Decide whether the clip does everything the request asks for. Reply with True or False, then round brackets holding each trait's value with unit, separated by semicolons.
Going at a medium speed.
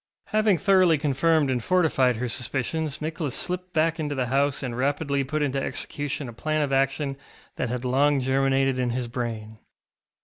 True (170 wpm)